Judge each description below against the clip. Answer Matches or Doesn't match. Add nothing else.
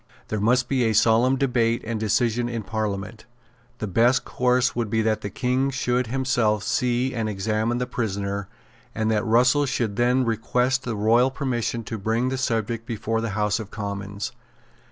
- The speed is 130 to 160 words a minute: Doesn't match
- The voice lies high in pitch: Doesn't match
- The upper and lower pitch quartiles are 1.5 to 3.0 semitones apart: Matches